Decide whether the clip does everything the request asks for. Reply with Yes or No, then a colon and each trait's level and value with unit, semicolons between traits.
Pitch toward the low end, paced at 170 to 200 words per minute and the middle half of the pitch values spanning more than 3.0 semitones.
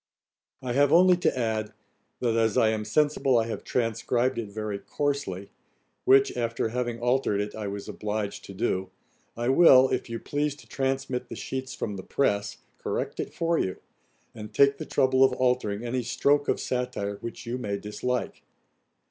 Yes: low, 120 Hz; average, 175 wpm; average, 3.7 semitones